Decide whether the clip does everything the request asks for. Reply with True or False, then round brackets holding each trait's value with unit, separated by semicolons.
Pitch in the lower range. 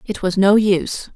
False (200 Hz)